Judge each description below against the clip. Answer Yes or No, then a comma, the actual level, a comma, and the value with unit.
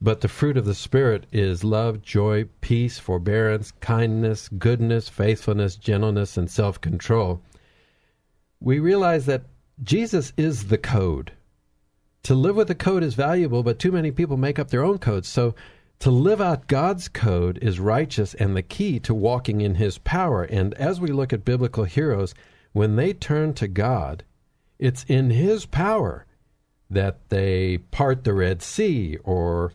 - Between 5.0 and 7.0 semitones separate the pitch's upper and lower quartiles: Yes, wide, 5.5 semitones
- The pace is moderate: Yes, average, 160 wpm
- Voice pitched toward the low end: Yes, low, 110 Hz